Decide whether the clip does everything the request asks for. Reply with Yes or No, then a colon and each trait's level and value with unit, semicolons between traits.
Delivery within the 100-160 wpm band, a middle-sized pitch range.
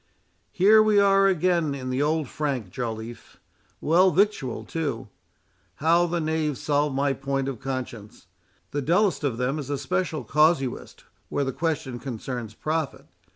Yes: average, 145 wpm; average, 4.2 semitones